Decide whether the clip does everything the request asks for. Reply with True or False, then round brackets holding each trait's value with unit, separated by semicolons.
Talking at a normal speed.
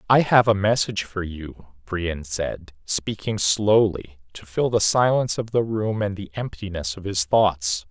True (175 wpm)